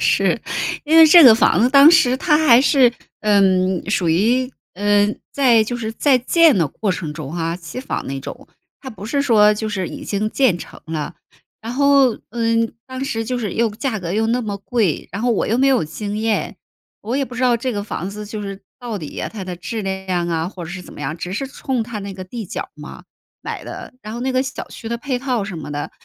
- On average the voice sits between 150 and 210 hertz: No, high, 220 Hz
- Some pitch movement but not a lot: Yes, average, 4.8 semitones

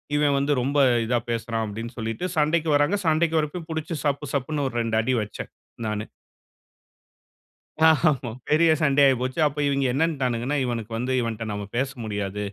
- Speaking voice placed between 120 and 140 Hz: Yes, low, 135 Hz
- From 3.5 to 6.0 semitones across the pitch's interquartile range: Yes, average, 4.6 semitones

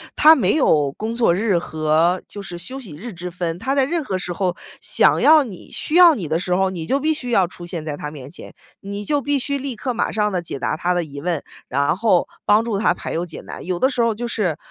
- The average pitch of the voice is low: No, high, 190 Hz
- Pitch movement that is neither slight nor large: No, wide, 6.3 semitones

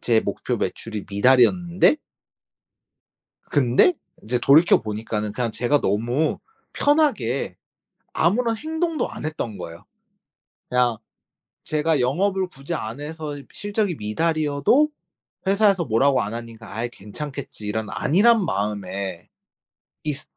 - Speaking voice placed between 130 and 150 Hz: Yes, low, 135 Hz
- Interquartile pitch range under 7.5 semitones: No, wide, 7.9 semitones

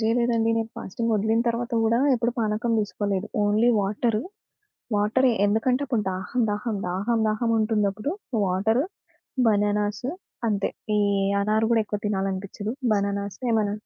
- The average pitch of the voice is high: Yes, high, 215 Hz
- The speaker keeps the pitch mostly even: Yes, narrow, 2.1 semitones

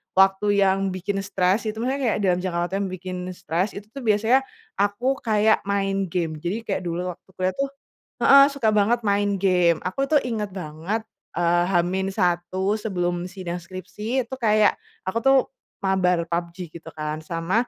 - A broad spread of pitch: No, average, 3.0 semitones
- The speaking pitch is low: No, high, 190 Hz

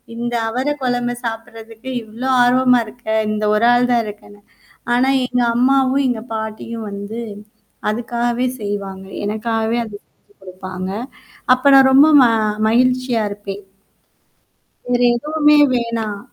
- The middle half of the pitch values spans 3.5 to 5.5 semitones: No, average, 2.8 semitones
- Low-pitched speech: No, high, 235 Hz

